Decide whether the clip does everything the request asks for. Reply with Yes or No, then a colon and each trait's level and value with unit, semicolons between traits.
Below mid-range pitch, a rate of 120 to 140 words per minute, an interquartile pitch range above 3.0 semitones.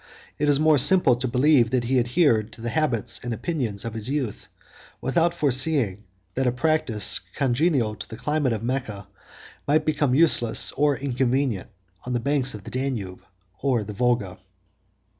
No: low, 125 Hz; average, 165 wpm; average, 4.2 semitones